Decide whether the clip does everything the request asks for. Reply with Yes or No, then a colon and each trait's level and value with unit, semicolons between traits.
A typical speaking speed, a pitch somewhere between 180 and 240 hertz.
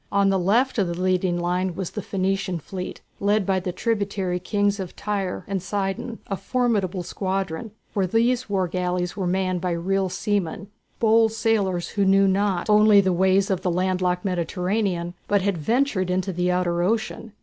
Yes: average, 180 wpm; high, 190 Hz